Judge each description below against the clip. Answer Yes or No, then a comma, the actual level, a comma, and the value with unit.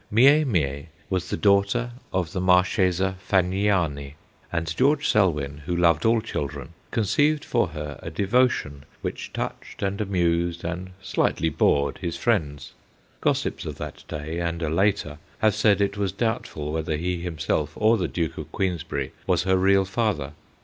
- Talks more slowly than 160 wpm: No, average, 165 wpm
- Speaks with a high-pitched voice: No, very low, 90 Hz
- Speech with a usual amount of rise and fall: Yes, average, 4.0 semitones